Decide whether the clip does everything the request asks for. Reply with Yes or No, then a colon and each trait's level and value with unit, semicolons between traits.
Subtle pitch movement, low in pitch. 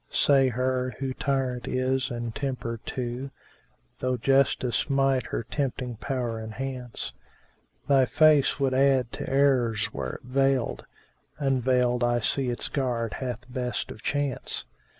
Yes: narrow, 1.9 semitones; low, 130 Hz